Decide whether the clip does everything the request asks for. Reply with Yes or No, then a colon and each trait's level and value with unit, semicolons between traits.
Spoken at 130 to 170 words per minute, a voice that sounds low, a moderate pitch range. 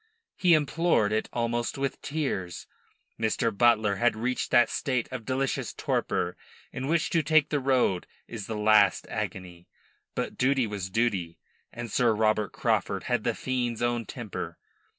Yes: average, 150 wpm; low, 120 Hz; average, 3.7 semitones